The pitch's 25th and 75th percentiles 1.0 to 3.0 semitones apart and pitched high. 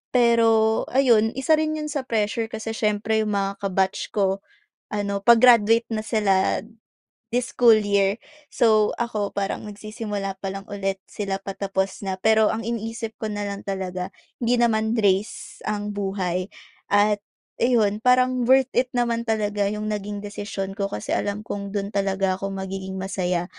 Yes: narrow, 2.4 semitones; high, 210 Hz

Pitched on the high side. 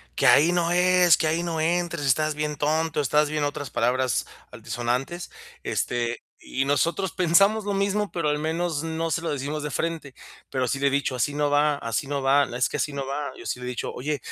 No: medium, 150 Hz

